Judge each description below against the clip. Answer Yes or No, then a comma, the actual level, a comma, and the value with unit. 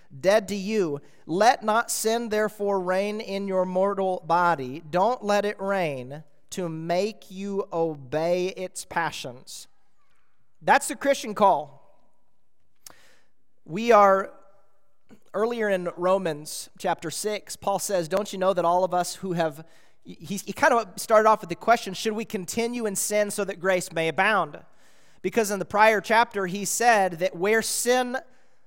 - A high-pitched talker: Yes, high, 195 Hz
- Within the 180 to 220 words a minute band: No, average, 155 wpm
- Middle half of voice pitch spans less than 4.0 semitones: Yes, average, 3.1 semitones